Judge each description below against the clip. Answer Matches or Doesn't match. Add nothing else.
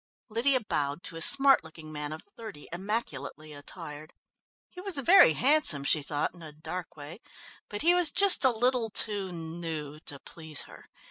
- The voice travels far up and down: Matches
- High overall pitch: Doesn't match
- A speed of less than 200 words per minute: Matches